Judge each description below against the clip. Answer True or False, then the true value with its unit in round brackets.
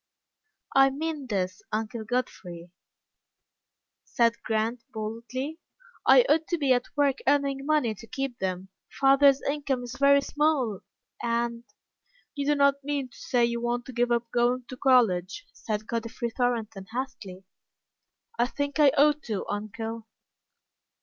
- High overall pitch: True (245 Hz)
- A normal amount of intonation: True (3.8 semitones)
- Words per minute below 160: True (140 wpm)